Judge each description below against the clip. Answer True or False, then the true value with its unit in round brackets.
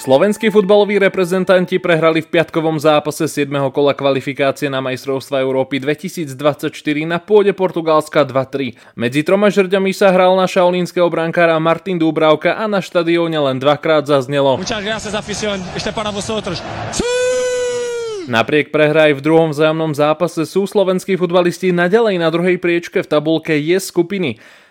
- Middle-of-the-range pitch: True (170 Hz)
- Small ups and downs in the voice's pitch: False (4.2 semitones)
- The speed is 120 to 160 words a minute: True (125 wpm)